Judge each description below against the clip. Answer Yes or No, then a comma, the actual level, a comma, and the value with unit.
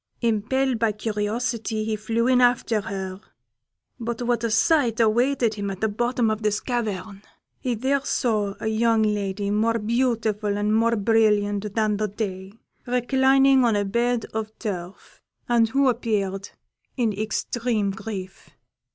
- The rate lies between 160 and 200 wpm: No, average, 145 wpm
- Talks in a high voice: Yes, high, 220 Hz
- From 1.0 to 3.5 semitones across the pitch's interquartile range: Yes, narrow, 2.5 semitones